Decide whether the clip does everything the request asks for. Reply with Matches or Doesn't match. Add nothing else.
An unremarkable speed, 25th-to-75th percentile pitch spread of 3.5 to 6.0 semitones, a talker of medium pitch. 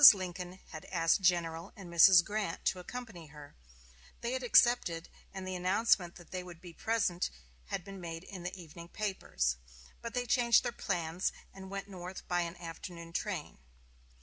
Doesn't match